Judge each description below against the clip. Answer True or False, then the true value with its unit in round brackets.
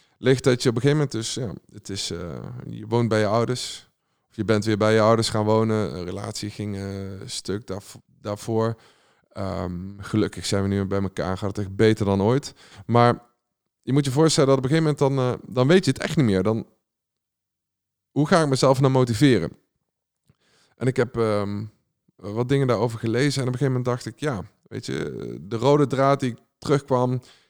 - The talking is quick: True (210 wpm)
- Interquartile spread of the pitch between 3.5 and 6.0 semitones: True (4.2 semitones)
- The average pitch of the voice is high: False (115 Hz)